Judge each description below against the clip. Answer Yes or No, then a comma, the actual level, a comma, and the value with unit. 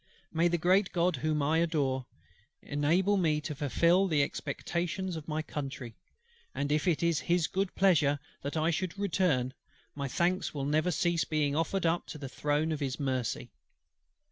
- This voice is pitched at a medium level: Yes, medium, 155 Hz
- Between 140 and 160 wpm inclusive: No, average, 170 wpm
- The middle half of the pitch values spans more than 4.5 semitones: No, average, 3.2 semitones